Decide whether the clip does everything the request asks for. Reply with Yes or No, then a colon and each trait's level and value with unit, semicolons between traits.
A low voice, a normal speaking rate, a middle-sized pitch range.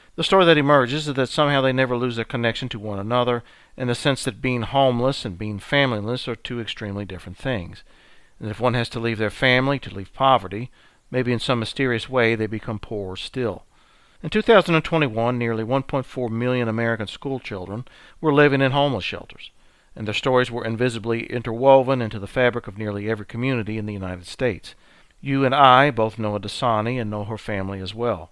Yes: low, 120 Hz; average, 195 wpm; average, 3.6 semitones